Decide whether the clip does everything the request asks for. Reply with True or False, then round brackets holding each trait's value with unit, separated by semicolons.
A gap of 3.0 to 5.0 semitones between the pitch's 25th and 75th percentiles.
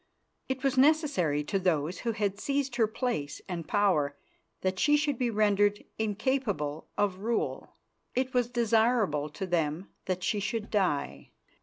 False (5.6 semitones)